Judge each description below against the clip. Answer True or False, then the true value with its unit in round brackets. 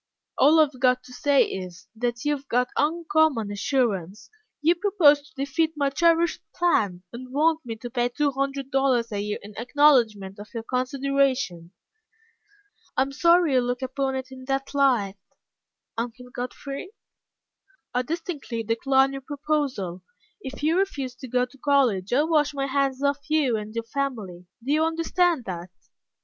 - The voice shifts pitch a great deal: False (3.7 semitones)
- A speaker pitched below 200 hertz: False (270 Hz)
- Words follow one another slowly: False (165 wpm)